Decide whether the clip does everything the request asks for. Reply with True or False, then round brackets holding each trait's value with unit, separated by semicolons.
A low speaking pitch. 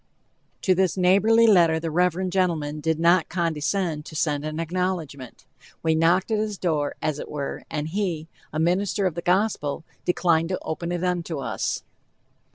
False (170 Hz)